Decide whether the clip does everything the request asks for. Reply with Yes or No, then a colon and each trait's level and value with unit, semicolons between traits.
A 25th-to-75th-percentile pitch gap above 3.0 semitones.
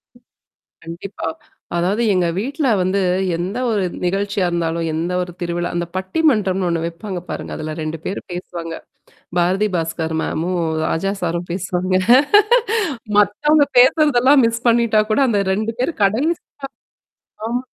Yes: average, 4.8 semitones